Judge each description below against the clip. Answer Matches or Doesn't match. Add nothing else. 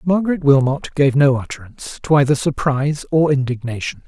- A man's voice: Matches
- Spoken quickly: Doesn't match